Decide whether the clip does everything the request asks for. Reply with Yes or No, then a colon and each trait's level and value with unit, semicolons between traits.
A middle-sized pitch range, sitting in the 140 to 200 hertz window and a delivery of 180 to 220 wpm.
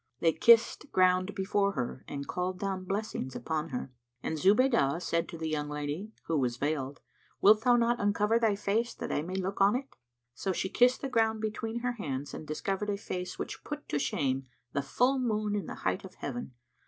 No: wide, 6.3 semitones; high, 190 Hz; fast, 205 wpm